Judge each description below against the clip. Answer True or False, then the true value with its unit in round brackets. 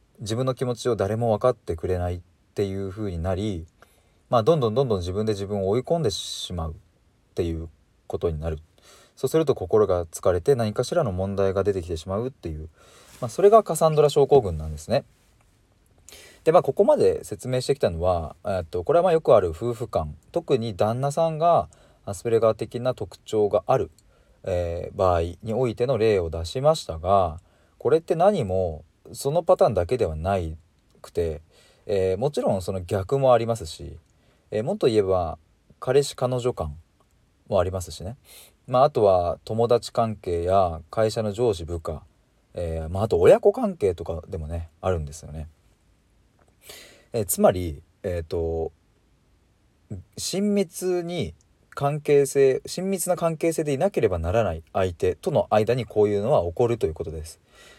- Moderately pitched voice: False (100 Hz)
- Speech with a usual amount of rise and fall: False (6.8 semitones)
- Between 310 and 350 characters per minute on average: True (330 characters per minute)